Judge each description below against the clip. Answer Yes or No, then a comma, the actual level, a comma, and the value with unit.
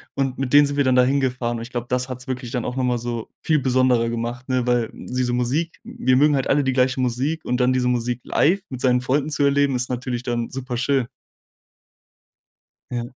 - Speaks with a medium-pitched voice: No, low, 125 Hz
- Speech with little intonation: Yes, narrow, 1.7 semitones